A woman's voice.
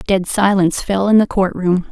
Yes: female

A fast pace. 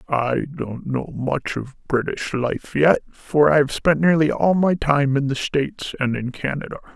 No: average, 190 wpm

